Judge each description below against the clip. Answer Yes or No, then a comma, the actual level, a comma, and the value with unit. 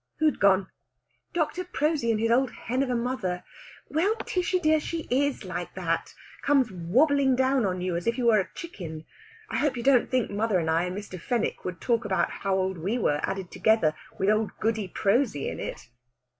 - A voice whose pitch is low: No, high, 230 Hz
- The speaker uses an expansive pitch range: Yes, wide, 6.2 semitones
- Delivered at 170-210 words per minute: Yes, average, 200 wpm